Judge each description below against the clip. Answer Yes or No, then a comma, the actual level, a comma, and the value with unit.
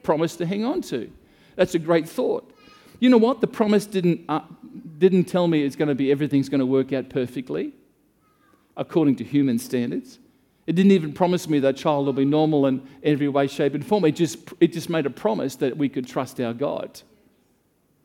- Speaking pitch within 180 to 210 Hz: No, medium, 155 Hz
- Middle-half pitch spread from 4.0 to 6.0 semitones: Yes, average, 4.8 semitones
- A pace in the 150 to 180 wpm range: No, fast, 205 wpm